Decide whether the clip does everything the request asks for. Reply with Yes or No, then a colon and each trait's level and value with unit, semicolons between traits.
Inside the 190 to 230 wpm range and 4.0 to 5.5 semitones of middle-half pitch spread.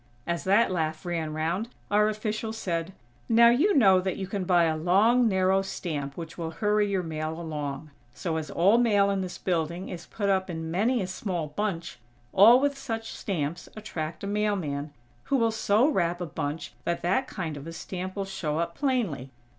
Yes: average, 195 wpm; average, 4.5 semitones